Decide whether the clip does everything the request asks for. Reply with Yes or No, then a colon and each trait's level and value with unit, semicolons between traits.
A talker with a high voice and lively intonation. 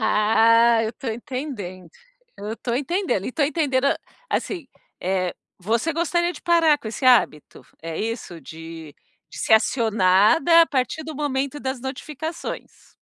Yes: very high, 250 Hz; wide, 6.0 semitones